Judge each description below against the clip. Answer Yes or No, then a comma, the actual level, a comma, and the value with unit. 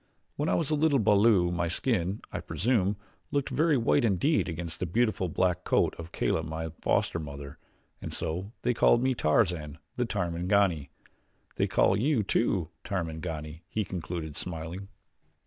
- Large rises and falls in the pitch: Yes, wide, 5.8 semitones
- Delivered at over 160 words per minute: No, average, 155 wpm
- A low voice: Yes, very low, 90 Hz